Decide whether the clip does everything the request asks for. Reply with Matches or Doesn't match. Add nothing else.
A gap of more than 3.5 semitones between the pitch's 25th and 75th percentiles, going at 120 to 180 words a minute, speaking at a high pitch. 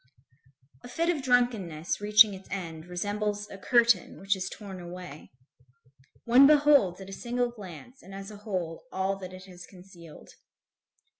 Matches